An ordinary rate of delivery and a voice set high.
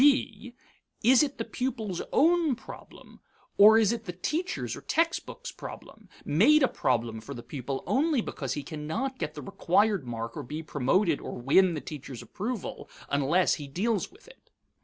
Yes: average, 170 wpm; high, 200 Hz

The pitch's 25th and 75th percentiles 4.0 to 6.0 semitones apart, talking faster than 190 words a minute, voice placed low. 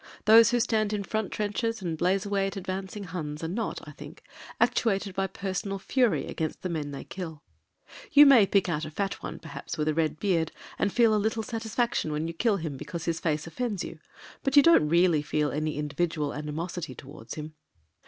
No: average, 5.2 semitones; fast, 205 wpm; medium, 185 Hz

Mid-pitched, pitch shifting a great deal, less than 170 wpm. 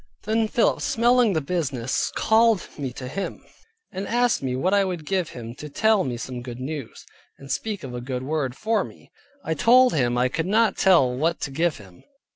No: medium, 160 Hz; wide, 8.8 semitones; average, 200 wpm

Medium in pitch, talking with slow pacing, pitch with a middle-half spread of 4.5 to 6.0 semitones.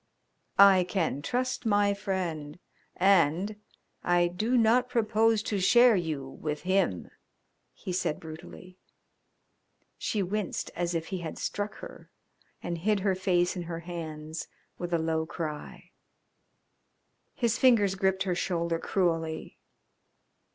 No: medium, 180 Hz; slow, 125 wpm; average, 3.7 semitones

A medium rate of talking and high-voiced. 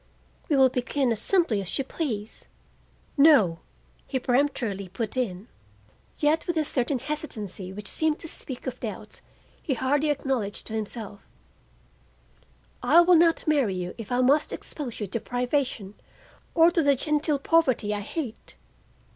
Yes: average, 150 wpm; very high, 255 Hz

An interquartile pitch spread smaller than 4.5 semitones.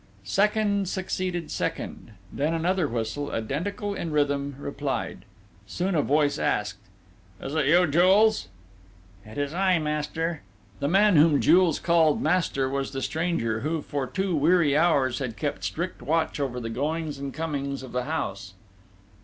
Yes: average, 4.0 semitones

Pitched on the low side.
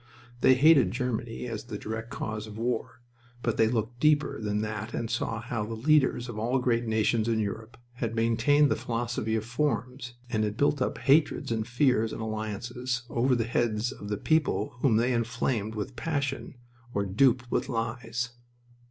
Yes: low, 115 Hz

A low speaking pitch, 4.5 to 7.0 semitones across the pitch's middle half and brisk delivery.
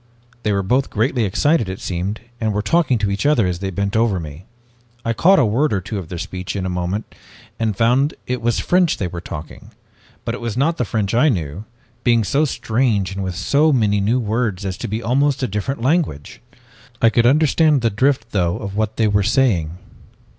Yes: low, 110 Hz; average, 4.9 semitones; fast, 215 wpm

